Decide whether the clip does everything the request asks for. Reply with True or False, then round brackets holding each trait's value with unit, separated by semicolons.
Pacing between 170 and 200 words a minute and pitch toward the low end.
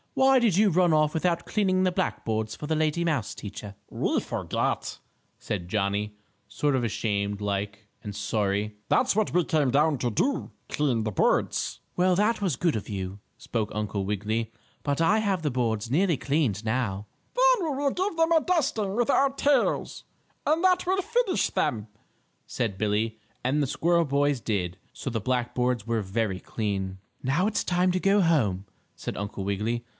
True (180 wpm; 130 Hz)